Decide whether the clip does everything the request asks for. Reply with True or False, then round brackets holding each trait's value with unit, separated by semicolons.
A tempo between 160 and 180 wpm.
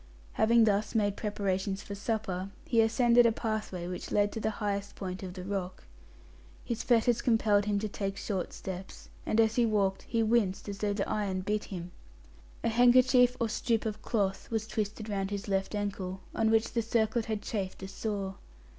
False (190 wpm)